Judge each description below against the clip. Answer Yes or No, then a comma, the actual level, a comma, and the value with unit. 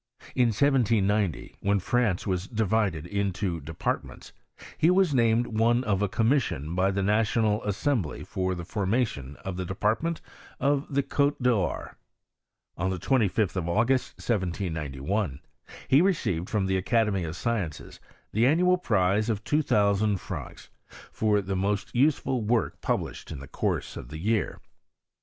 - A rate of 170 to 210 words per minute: No, average, 145 wpm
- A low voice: Yes, low, 105 Hz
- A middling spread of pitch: Yes, average, 4.3 semitones